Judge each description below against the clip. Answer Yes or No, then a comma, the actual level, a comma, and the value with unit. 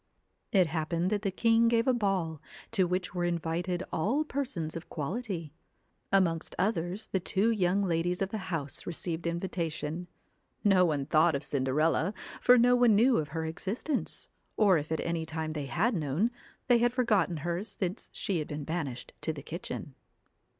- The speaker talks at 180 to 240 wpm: No, average, 170 wpm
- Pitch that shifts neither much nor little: Yes, average, 4.4 semitones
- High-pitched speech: No, medium, 175 Hz